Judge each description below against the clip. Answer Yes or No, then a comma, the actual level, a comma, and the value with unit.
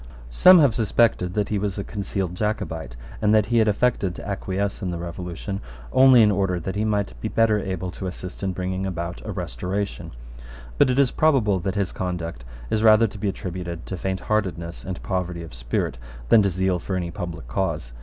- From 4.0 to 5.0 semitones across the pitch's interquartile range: No, average, 3.1 semitones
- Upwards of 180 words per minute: Yes, average, 200 wpm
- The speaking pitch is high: No, very low, 95 Hz